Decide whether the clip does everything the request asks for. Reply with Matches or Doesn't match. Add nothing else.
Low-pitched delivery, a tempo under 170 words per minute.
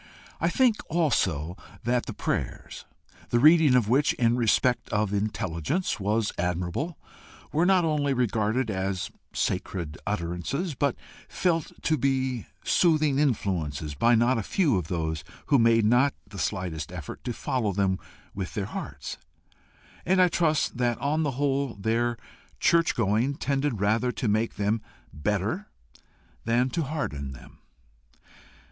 Matches